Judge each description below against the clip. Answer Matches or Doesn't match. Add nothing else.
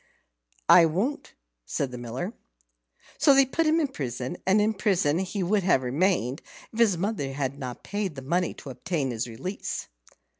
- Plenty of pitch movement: Matches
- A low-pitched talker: Doesn't match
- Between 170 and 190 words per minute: Matches